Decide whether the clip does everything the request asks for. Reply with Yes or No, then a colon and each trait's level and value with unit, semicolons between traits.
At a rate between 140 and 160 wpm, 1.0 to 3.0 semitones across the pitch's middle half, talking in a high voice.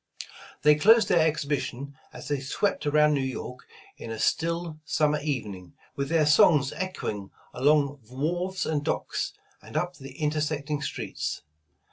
No: average, 145 wpm; narrow, 2.5 semitones; medium, 150 Hz